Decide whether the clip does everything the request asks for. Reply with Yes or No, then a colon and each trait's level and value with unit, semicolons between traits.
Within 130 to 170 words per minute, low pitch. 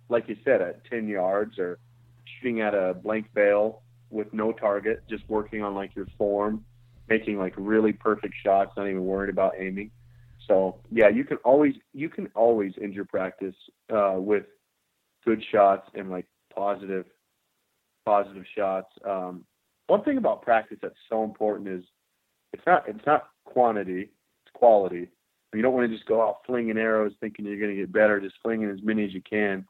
No: average, 180 wpm; low, 105 Hz